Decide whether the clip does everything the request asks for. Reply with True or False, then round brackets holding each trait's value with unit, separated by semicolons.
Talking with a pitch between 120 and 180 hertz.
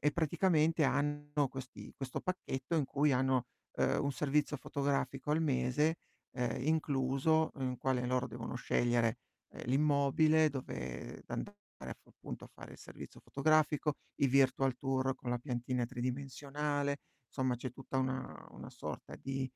True (135 Hz)